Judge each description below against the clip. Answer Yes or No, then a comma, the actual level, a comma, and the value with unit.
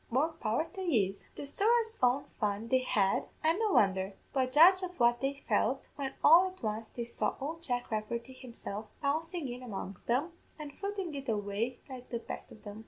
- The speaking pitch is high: Yes, very high, 255 Hz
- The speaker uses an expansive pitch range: Yes, wide, 6.3 semitones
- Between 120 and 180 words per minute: No, average, 195 wpm